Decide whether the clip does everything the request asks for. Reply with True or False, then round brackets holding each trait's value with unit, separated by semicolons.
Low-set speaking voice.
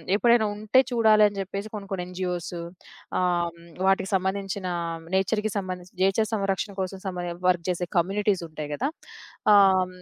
False (190 Hz)